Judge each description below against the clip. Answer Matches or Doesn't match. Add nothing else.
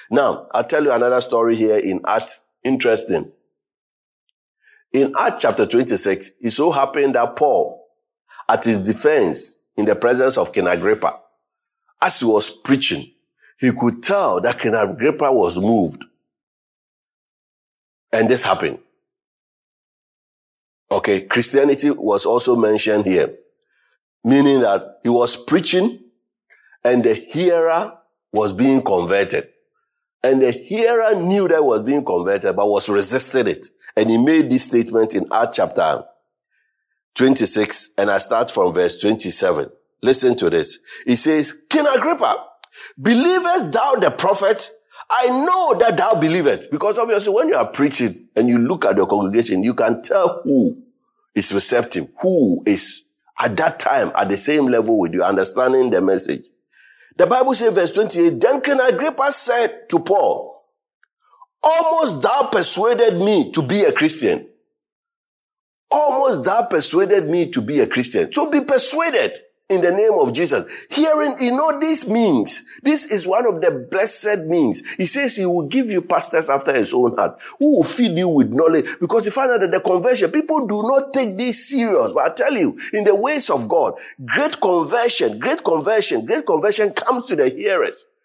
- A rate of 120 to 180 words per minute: Matches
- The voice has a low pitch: Doesn't match